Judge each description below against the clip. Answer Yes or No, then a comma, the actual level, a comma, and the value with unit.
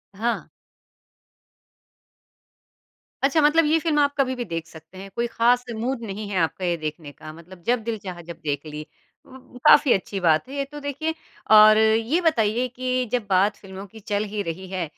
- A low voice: No, high, 215 Hz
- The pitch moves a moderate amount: No, wide, 5.9 semitones